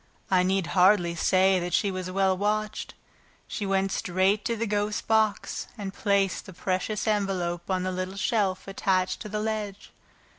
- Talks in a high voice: Yes, high, 195 Hz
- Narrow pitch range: Yes, narrow, 2.1 semitones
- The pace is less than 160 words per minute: No, average, 170 wpm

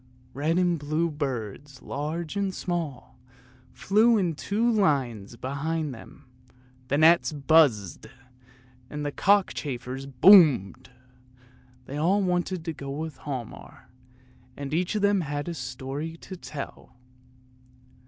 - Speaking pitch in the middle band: Yes, medium, 150 Hz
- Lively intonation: No, average, 4.3 semitones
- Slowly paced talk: Yes, slow, 125 wpm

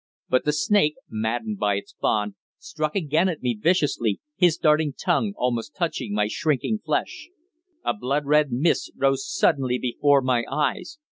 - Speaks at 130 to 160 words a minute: Yes, average, 155 wpm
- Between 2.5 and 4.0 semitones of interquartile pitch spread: No, average, 4.6 semitones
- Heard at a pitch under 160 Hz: Yes, medium, 140 Hz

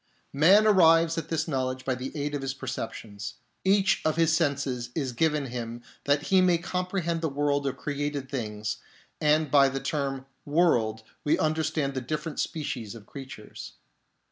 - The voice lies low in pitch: No, medium, 145 Hz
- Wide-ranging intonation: No, average, 3.7 semitones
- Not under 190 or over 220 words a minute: No, average, 170 wpm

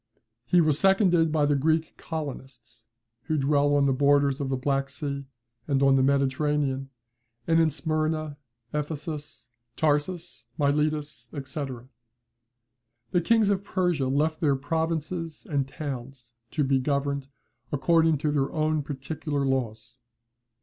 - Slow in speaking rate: Yes, slow, 130 wpm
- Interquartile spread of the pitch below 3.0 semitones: Yes, narrow, 2.6 semitones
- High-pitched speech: No, medium, 145 Hz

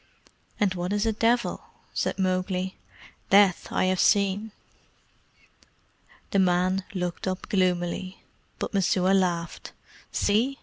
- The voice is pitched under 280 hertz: Yes, high, 190 Hz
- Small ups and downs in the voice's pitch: Yes, narrow, 1.9 semitones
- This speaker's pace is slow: Yes, slow, 115 wpm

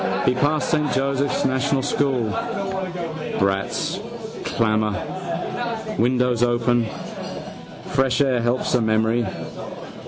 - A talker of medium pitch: No, low, 125 Hz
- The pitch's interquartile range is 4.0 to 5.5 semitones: No, average, 2.9 semitones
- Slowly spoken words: Yes, slow, 85 wpm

